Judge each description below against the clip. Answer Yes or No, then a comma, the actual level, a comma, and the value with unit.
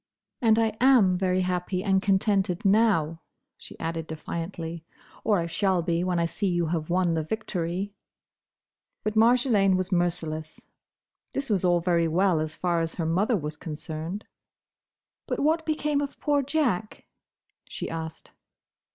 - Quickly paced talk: No, average, 145 wpm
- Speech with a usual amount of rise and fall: Yes, average, 4.3 semitones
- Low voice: No, medium, 180 Hz